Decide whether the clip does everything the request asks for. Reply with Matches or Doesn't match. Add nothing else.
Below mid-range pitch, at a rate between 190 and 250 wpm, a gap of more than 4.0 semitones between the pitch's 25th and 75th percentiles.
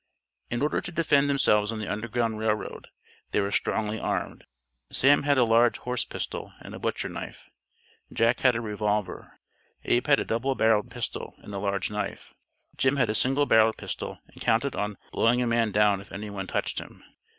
Doesn't match